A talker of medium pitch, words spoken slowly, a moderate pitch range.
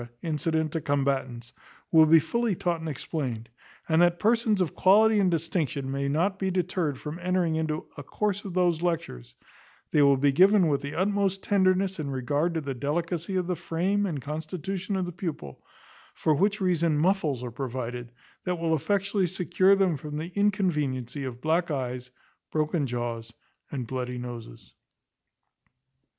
No: medium, 160 Hz; average, 165 wpm; average, 5.0 semitones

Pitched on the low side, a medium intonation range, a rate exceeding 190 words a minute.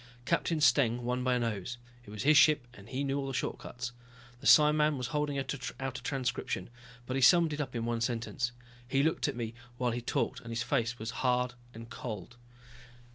Yes: low, 125 Hz; average, 3.0 semitones; fast, 205 wpm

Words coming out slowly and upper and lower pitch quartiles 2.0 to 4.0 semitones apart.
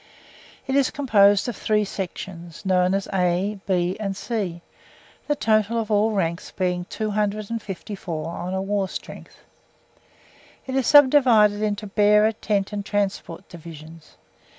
Yes: slow, 130 wpm; average, 2.9 semitones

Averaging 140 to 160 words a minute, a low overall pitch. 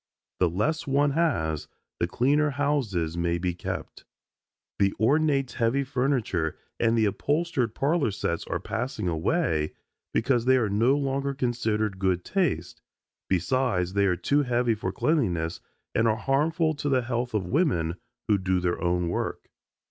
Yes: average, 150 wpm; low, 115 Hz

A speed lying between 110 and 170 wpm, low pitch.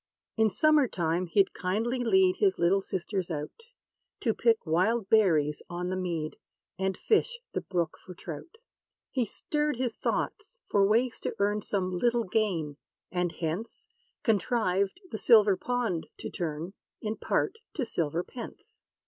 No: average, 150 wpm; high, 200 Hz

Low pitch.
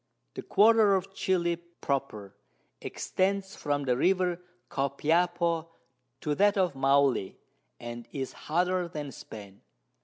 No: medium, 165 Hz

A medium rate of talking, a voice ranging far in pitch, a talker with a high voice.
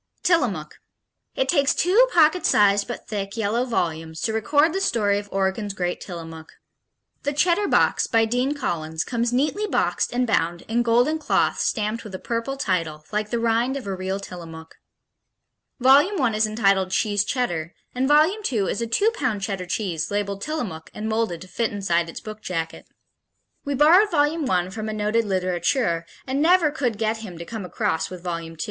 Yes: average, 185 wpm; wide, 6.3 semitones; high, 220 Hz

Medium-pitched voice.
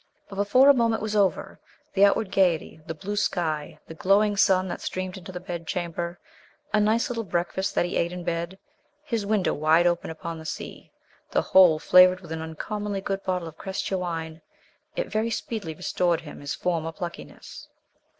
Yes: medium, 180 Hz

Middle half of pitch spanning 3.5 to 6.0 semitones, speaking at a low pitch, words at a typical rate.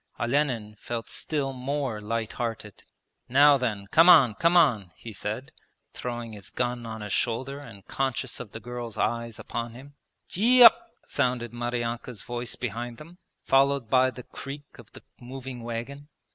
No: average, 3.0 semitones; low, 120 Hz; average, 160 wpm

